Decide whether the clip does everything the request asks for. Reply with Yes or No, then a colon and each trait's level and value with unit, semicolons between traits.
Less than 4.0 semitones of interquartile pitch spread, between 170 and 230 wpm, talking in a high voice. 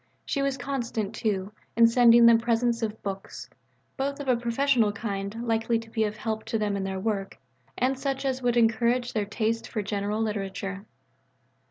Yes: narrow, 2.6 semitones; average, 180 wpm; high, 225 Hz